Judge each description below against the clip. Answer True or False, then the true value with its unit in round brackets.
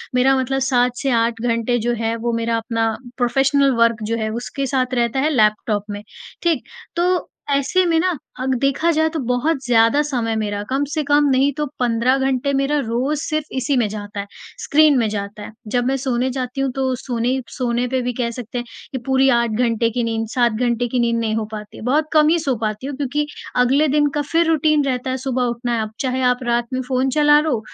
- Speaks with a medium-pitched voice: False (250 Hz)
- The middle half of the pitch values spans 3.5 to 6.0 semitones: False (3.1 semitones)